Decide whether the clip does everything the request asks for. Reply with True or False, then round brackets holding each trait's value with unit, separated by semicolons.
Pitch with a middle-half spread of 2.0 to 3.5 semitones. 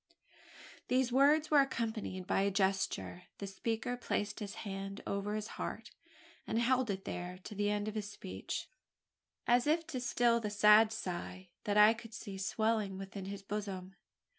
True (3.1 semitones)